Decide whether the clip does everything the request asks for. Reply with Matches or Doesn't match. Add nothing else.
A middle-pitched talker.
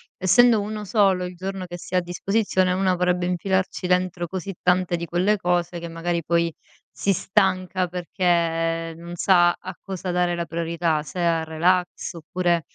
Matches